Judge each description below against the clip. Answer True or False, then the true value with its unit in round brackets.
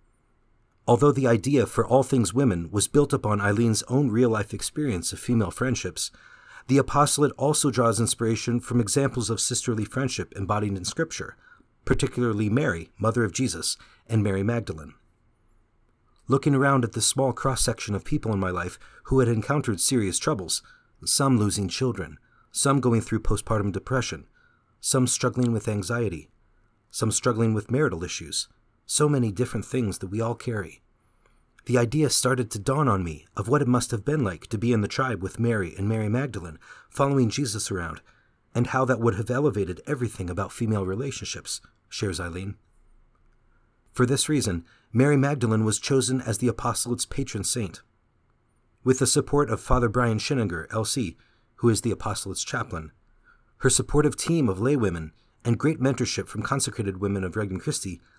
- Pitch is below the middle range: True (115 Hz)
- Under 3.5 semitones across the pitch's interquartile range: False (3.9 semitones)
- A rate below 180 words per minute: True (165 wpm)